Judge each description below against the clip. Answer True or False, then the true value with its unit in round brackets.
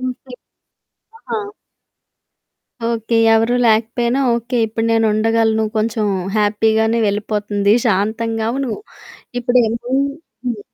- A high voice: True (225 Hz)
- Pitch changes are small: True (1.8 semitones)